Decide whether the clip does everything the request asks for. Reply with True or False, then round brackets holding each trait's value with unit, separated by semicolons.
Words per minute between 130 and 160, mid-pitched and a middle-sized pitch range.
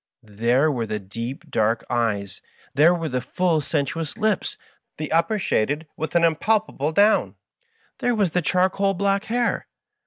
False (150 wpm; 160 Hz; 8.1 semitones)